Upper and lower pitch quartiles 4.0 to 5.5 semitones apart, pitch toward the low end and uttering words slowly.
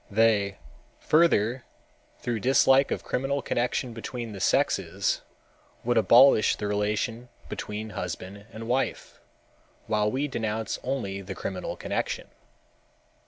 No: average, 3.3 semitones; low, 115 Hz; slow, 115 wpm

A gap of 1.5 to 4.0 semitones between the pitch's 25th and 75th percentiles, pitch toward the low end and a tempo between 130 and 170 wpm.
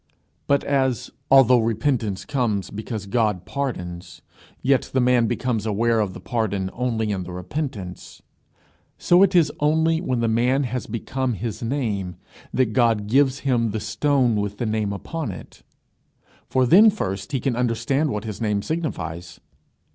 No: average, 4.4 semitones; low, 115 Hz; average, 155 wpm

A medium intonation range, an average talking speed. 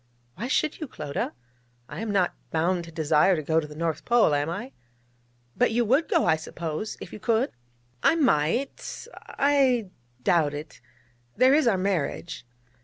No: wide, 7.6 semitones; average, 170 wpm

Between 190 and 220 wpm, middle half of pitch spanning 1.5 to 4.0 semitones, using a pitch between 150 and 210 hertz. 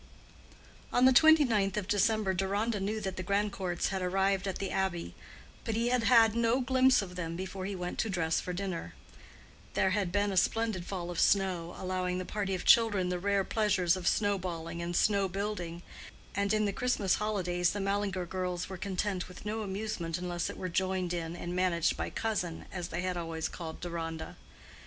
Yes: average, 195 wpm; average, 2.7 semitones; high, 190 Hz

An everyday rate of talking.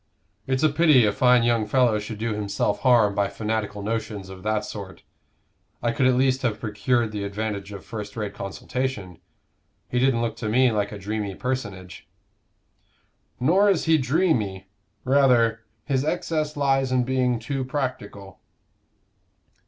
Yes: average, 150 wpm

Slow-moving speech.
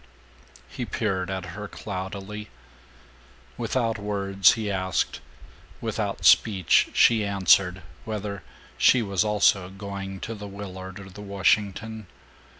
Yes: slow, 115 wpm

